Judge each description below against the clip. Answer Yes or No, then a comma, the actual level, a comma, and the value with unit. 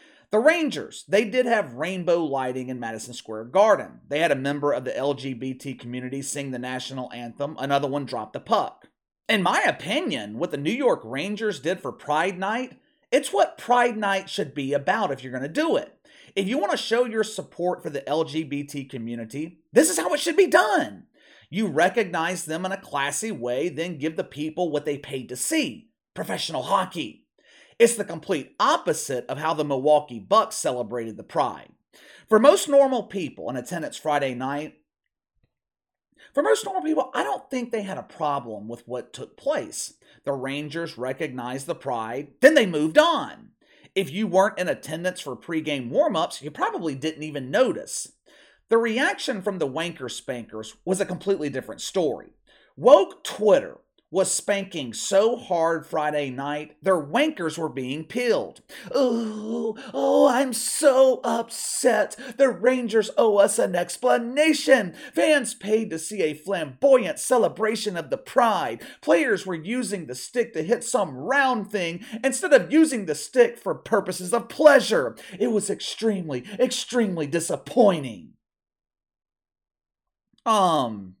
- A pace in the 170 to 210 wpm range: No, average, 160 wpm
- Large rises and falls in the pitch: Yes, wide, 8.9 semitones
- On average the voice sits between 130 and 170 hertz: No, medium, 185 Hz